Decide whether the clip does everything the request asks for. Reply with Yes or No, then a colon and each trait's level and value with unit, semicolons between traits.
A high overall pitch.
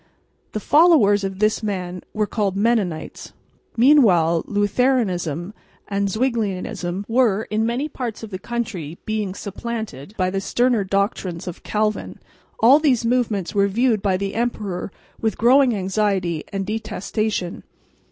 Yes: high, 210 Hz